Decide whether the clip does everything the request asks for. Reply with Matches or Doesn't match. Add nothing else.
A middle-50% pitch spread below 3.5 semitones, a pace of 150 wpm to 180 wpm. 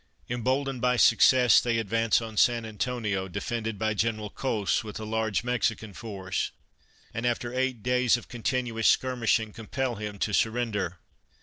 Matches